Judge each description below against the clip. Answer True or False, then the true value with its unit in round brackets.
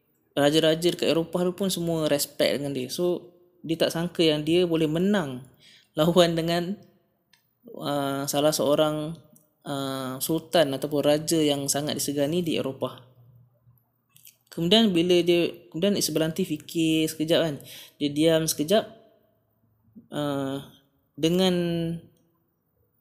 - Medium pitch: True (155 Hz)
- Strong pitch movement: False (3.7 semitones)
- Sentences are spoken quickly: False (110 wpm)